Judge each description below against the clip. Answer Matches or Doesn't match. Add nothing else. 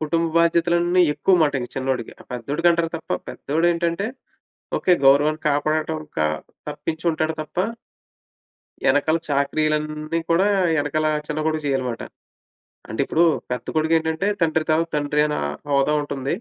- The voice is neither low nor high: Matches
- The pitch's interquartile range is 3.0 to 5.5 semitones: Doesn't match